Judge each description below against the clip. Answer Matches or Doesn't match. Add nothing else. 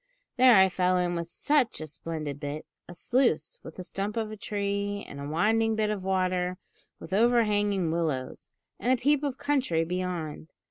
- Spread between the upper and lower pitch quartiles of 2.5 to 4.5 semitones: Doesn't match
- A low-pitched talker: Doesn't match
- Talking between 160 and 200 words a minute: Matches